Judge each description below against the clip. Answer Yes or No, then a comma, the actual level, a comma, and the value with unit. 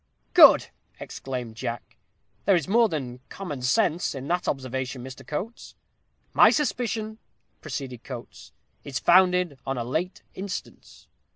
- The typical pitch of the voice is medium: Yes, medium, 145 Hz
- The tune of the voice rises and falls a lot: Yes, wide, 6.6 semitones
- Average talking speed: No, slow, 130 wpm